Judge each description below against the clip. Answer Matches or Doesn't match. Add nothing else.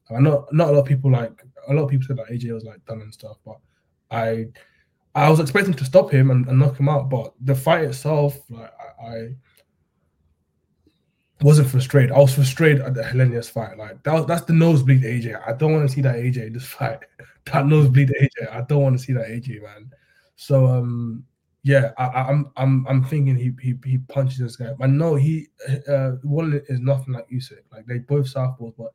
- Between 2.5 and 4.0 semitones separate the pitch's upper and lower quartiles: Matches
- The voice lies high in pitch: Doesn't match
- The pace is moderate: Doesn't match